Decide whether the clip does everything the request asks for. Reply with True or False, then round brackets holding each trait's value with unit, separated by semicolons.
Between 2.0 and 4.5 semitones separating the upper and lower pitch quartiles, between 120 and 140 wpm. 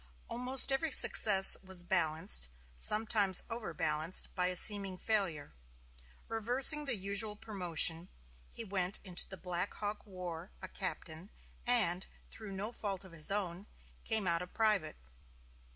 True (3.5 semitones; 135 wpm)